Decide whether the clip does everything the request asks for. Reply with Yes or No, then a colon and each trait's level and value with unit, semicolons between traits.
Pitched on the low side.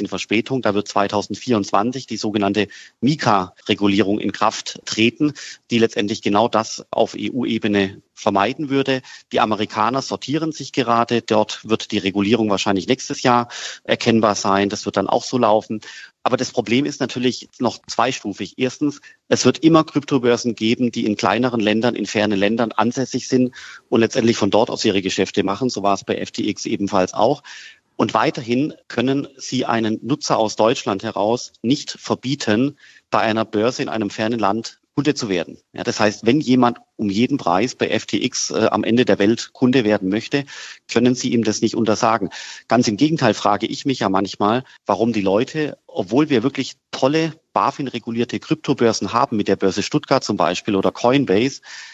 Yes: low, 115 Hz